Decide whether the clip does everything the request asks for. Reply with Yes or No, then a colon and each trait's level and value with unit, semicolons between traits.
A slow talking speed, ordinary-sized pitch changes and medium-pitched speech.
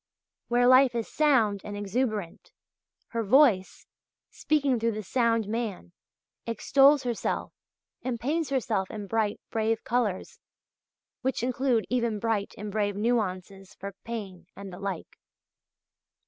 No: slow, 125 wpm; average, 3.5 semitones; high, 225 Hz